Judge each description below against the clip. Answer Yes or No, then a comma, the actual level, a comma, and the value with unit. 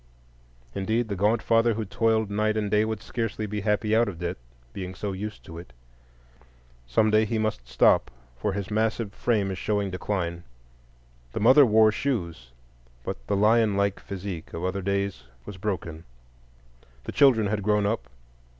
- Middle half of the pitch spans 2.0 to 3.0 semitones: Yes, average, 2.7 semitones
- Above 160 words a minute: Yes, average, 170 wpm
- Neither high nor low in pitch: No, low, 105 Hz